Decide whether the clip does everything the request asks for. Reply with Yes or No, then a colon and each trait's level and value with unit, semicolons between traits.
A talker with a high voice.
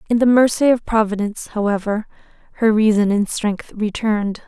Yes: high, 215 Hz